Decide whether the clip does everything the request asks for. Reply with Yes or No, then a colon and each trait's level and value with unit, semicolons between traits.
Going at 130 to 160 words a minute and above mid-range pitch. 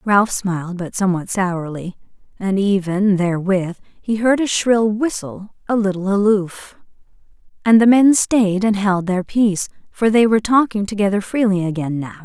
Yes: average, 155 wpm; high, 200 Hz